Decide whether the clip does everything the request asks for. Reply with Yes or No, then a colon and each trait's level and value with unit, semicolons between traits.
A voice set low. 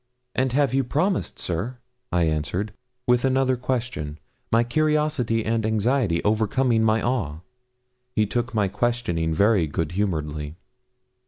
Yes: low, 110 Hz